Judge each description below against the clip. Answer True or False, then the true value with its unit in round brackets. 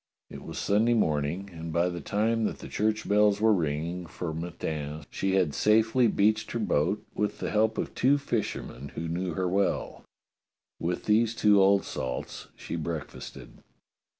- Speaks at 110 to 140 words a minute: False (170 wpm)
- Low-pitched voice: True (95 Hz)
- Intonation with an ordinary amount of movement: True (4.6 semitones)